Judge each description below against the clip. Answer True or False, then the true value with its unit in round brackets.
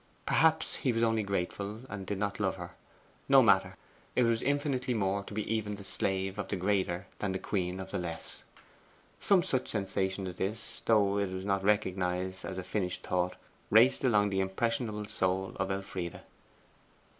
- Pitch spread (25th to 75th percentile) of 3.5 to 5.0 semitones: False (2.5 semitones)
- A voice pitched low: True (100 Hz)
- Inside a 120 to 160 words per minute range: False (180 wpm)